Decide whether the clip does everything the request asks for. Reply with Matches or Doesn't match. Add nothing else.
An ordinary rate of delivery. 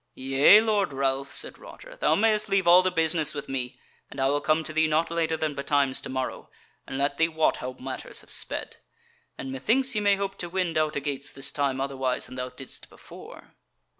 Doesn't match